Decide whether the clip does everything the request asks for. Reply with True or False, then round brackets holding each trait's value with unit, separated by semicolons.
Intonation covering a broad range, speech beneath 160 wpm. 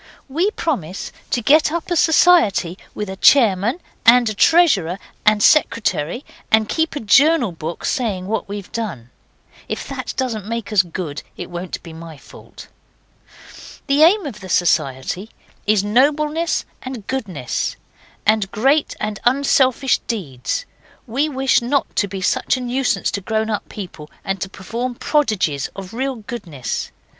True (6.2 semitones; 150 wpm)